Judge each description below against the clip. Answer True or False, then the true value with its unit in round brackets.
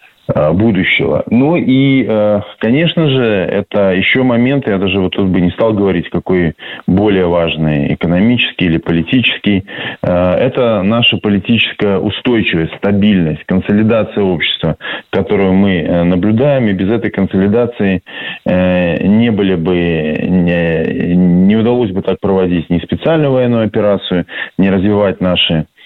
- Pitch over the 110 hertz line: False (95 Hz)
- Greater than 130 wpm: False (120 wpm)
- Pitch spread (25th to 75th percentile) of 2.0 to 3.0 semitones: False (3.6 semitones)